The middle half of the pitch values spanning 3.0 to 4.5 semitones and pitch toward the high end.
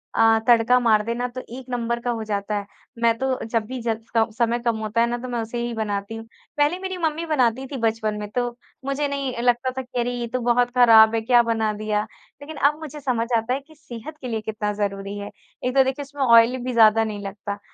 No: narrow, 2.6 semitones; high, 235 Hz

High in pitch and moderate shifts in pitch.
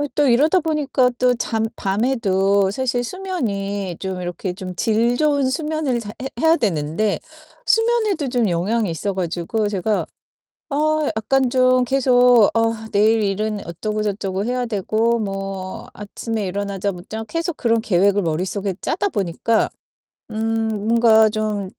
Yes: high, 220 Hz; average, 4.3 semitones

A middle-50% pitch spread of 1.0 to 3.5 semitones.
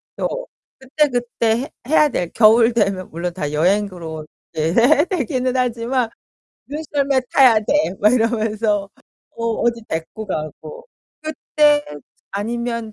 No: average, 5.3 semitones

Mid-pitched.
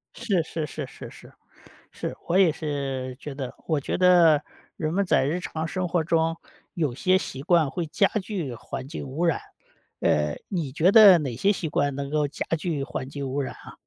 Yes: medium, 155 Hz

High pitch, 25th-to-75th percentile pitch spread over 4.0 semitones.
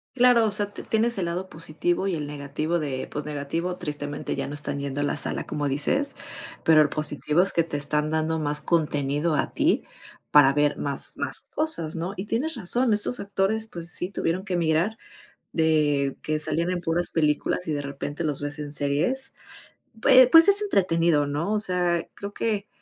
No: medium, 165 Hz; average, 5.0 semitones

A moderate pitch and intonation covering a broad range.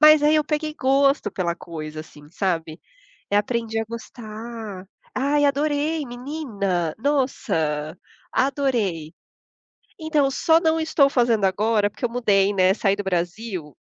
No: high, 225 Hz; wide, 7.1 semitones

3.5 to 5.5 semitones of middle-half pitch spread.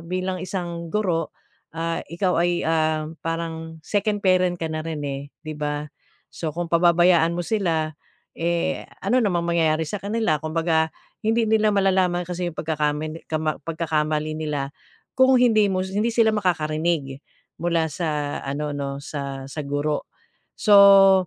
No: average, 3.1 semitones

